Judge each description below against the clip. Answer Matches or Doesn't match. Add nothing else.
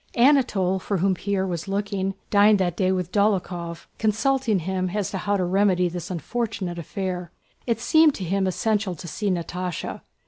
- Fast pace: Doesn't match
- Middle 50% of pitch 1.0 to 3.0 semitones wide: Matches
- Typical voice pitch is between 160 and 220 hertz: Matches